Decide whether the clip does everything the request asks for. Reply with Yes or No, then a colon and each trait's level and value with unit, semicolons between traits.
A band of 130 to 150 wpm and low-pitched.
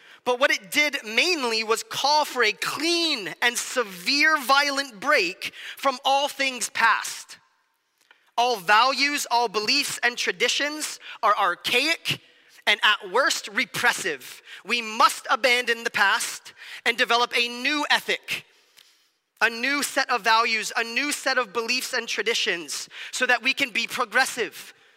No: average, 140 wpm; very high, 260 Hz